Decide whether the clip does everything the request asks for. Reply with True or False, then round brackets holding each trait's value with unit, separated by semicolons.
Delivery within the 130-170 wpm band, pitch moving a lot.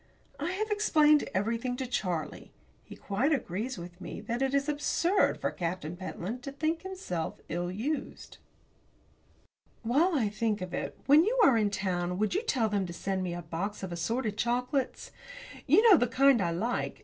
False (180 wpm; 7.6 semitones)